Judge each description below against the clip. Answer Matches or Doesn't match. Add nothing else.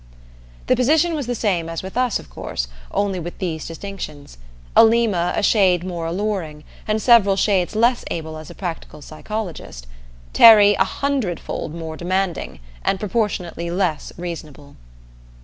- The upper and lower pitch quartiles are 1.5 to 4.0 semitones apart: Doesn't match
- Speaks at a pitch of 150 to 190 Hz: Matches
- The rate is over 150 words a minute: Doesn't match